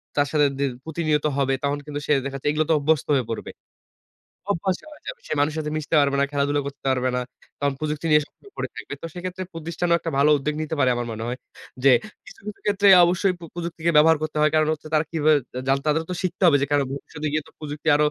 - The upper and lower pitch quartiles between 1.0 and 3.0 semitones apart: Yes, narrow, 2.6 semitones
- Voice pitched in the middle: Yes, medium, 150 Hz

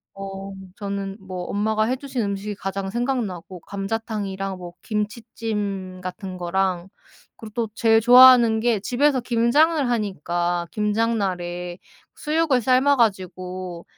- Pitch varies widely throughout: No, average, 3.8 semitones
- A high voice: Yes, high, 205 Hz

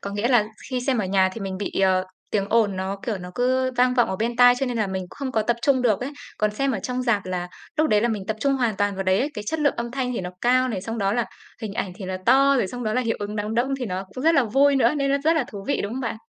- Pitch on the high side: Yes, high, 230 Hz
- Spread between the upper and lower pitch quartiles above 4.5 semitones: No, average, 4.2 semitones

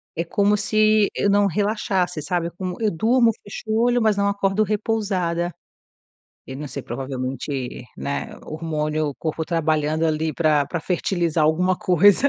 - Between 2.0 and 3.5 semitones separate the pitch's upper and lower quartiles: No, average, 4.8 semitones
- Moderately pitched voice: Yes, medium, 175 Hz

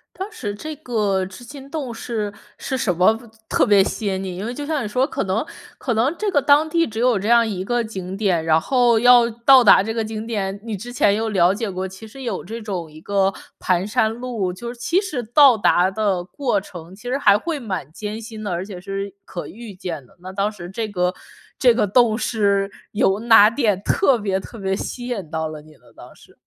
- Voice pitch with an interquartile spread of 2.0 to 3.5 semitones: No, average, 4.1 semitones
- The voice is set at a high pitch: Yes, high, 215 Hz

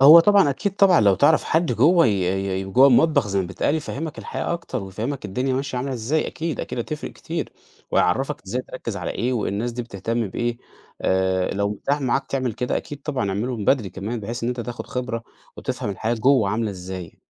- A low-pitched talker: Yes, low, 120 Hz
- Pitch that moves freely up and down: Yes, wide, 5.7 semitones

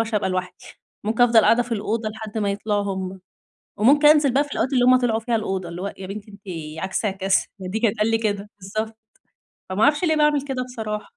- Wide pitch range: No, average, 3.5 semitones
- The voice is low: No, high, 220 Hz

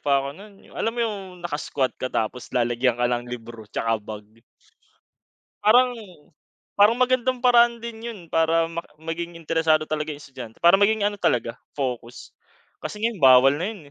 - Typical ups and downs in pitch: No, wide, 9.0 semitones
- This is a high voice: No, medium, 165 Hz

